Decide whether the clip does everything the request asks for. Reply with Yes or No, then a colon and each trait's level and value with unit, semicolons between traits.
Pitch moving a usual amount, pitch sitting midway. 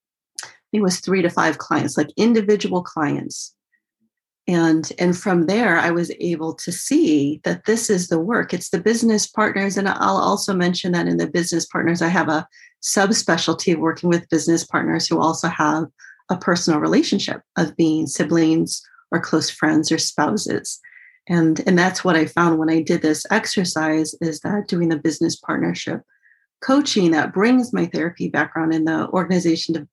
Yes: average, 3.5 semitones; medium, 170 Hz